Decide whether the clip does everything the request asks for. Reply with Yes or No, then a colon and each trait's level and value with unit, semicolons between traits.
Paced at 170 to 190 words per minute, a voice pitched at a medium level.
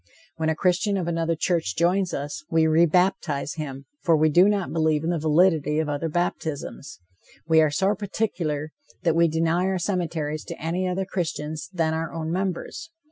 Yes: average, 185 wpm; medium, 165 Hz